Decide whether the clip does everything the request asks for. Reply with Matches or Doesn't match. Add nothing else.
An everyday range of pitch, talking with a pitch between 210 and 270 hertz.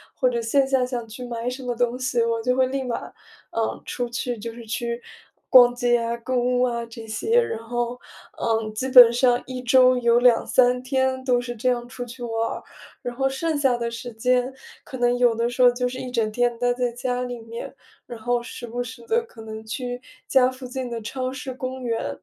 Doesn't match